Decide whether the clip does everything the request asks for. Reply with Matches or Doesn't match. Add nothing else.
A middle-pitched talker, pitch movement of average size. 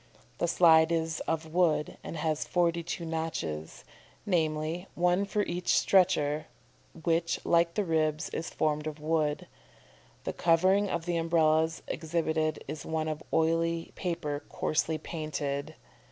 Doesn't match